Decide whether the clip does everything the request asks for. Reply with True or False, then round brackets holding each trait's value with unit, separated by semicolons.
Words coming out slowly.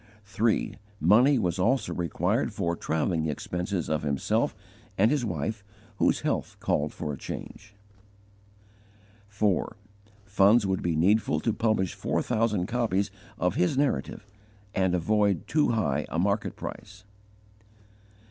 True (130 wpm)